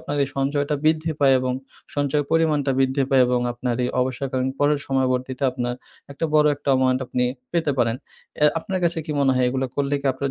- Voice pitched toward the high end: No, low, 135 Hz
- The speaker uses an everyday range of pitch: No, narrow, 2.2 semitones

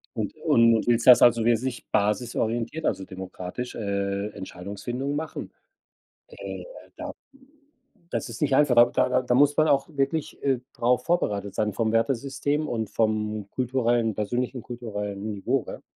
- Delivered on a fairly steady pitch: No, average, 3.7 semitones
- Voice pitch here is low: Yes, low, 120 Hz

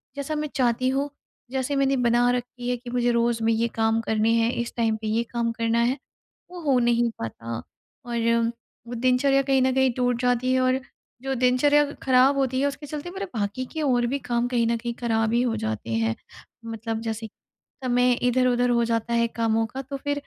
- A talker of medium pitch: No, high, 245 Hz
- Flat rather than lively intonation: Yes, narrow, 2.3 semitones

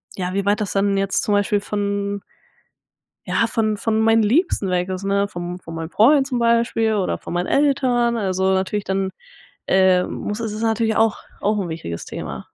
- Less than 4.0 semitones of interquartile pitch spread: Yes, average, 2.9 semitones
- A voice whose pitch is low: No, high, 205 Hz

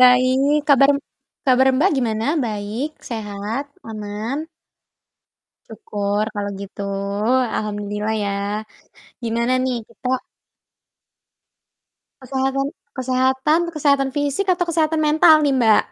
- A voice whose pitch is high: Yes, very high, 260 Hz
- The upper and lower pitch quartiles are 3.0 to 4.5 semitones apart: No, average, 4.9 semitones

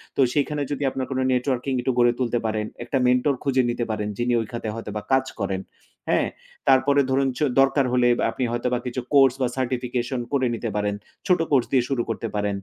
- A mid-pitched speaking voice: No, low, 125 Hz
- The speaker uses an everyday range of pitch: No, narrow, 2.1 semitones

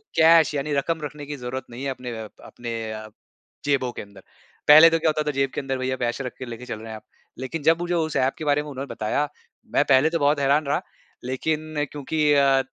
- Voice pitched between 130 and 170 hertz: Yes, medium, 140 Hz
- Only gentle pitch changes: No, average, 3.1 semitones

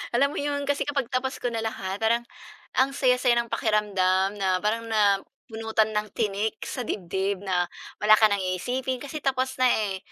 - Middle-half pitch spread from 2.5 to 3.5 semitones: No, average, 4.3 semitones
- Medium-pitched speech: No, high, 220 Hz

